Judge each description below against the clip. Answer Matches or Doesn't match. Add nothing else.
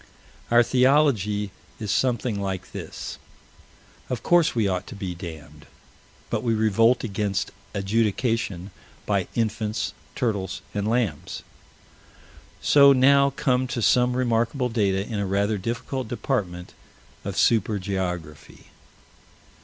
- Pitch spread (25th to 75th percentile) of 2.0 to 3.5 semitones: Doesn't match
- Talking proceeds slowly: Matches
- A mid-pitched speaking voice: Doesn't match